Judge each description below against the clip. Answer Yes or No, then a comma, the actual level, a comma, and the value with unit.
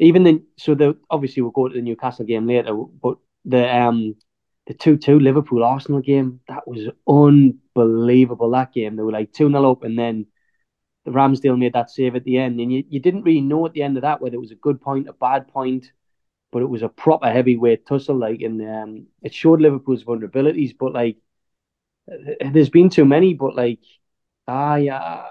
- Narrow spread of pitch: No, average, 3.4 semitones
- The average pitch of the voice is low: Yes, low, 130 Hz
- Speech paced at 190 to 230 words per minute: Yes, fast, 205 wpm